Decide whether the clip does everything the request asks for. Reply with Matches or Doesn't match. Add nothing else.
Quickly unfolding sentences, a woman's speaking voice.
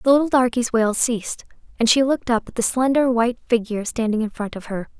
Matches